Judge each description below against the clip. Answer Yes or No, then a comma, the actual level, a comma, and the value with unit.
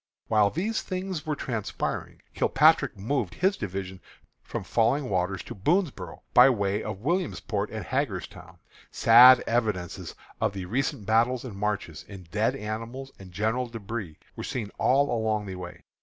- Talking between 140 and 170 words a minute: Yes, average, 150 wpm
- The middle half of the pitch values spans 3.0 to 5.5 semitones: Yes, average, 5.2 semitones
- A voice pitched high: No, low, 110 Hz